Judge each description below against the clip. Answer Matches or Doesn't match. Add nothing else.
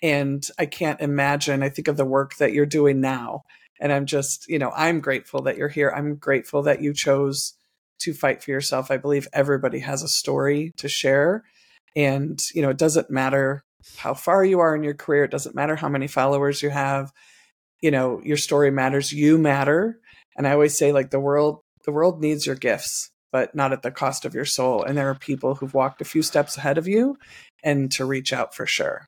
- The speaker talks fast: Matches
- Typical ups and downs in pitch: Doesn't match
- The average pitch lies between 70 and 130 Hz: Doesn't match